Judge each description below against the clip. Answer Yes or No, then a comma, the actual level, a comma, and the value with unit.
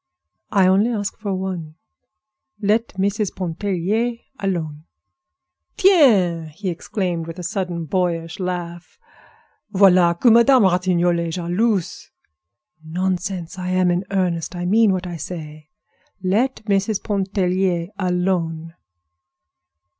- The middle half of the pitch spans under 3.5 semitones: Yes, narrow, 2.6 semitones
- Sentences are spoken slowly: Yes, slow, 110 wpm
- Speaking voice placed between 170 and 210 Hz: Yes, medium, 185 Hz